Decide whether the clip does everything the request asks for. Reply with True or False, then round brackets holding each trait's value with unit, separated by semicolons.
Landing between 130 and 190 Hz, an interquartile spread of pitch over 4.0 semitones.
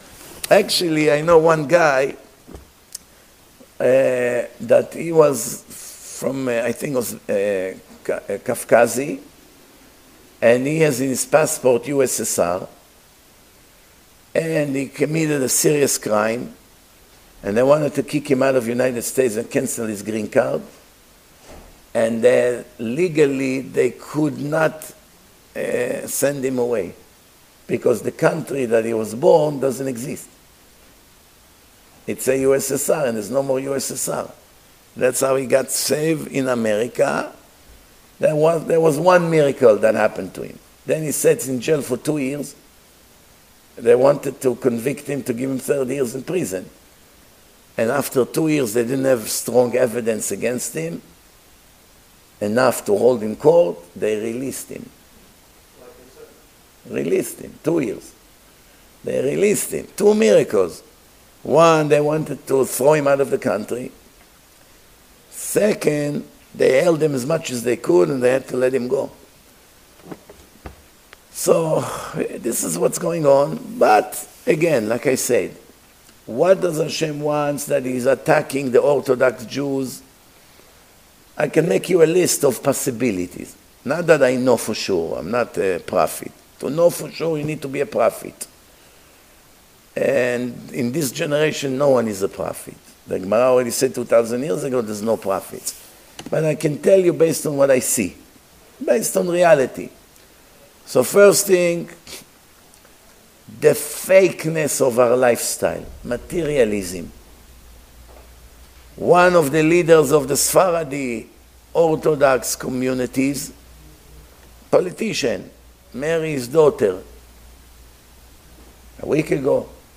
True (135 Hz; 4.8 semitones)